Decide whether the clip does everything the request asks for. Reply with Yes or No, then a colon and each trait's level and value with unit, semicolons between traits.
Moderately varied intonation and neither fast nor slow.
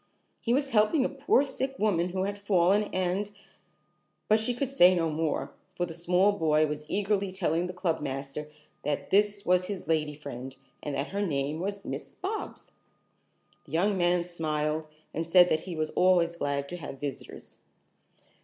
Yes: average, 4.6 semitones; average, 175 wpm